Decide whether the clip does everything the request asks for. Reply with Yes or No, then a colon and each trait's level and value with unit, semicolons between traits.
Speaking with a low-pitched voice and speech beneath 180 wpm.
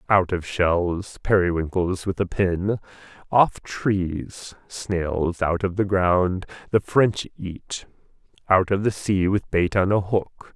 Yes: very low, 95 Hz; average, 150 wpm